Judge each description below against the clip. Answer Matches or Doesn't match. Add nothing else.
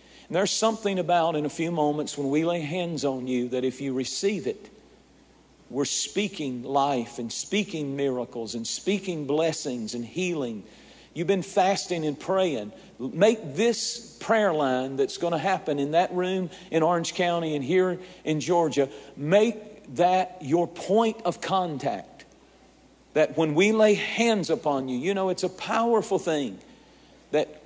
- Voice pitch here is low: Doesn't match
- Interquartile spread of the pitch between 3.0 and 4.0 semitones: Doesn't match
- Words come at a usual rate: Matches